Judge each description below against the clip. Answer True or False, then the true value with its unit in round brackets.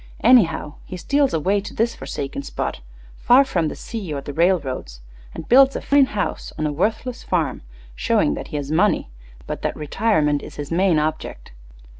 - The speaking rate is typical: True (180 wpm)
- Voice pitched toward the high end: False (170 Hz)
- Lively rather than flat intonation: True (7.2 semitones)